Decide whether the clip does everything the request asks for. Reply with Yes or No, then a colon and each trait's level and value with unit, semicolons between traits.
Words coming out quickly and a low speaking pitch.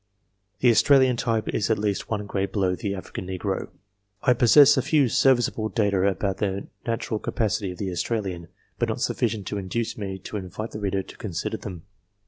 No: average, 185 wpm; low, 105 Hz